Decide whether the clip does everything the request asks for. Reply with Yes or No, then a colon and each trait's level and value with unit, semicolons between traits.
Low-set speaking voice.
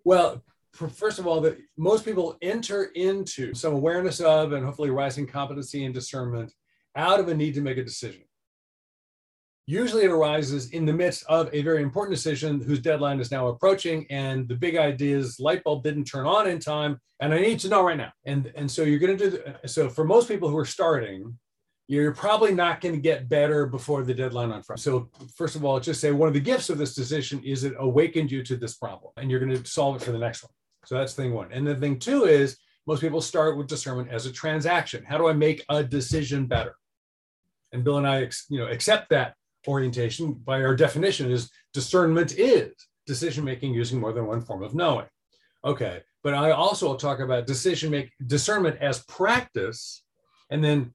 No: medium, 145 Hz